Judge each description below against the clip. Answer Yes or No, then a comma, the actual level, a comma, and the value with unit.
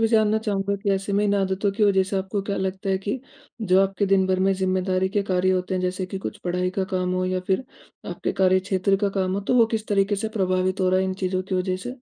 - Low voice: No, high, 190 Hz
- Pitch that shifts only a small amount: Yes, narrow, 1.3 semitones